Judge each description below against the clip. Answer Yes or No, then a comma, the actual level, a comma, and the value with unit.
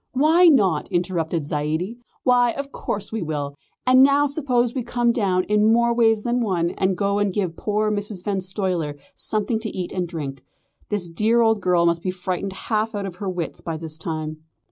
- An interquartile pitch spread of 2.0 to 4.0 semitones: No, average, 5.1 semitones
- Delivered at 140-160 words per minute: No, average, 195 wpm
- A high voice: Yes, high, 200 Hz